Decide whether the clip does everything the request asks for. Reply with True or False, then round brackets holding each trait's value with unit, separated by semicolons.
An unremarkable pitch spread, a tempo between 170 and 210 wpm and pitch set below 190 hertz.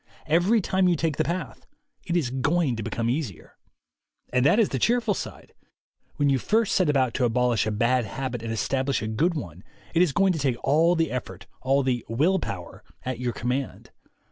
False (5.7 semitones; 200 wpm; 135 Hz)